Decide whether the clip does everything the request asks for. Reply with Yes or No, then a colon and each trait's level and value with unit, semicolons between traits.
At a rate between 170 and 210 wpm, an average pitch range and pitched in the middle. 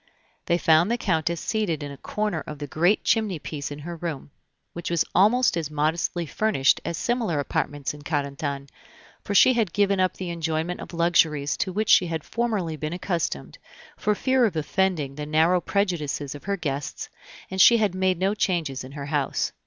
Yes: average, 190 wpm; average, 4.7 semitones; medium, 170 Hz